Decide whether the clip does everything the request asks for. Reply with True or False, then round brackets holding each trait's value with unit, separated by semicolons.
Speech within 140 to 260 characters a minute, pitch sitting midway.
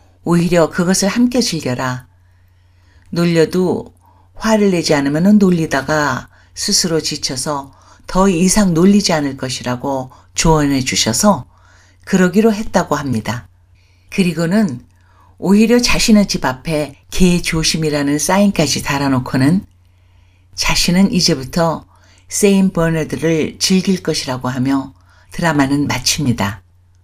True (255 characters per minute; 150 Hz)